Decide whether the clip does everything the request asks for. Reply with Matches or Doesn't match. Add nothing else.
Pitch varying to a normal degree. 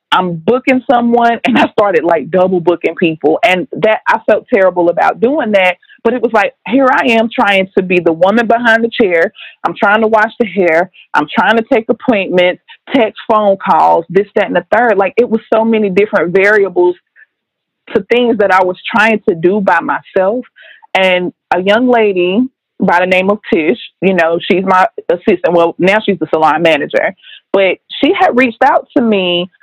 Matches